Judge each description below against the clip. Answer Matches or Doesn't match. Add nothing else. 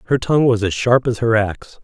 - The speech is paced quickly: Matches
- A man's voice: Matches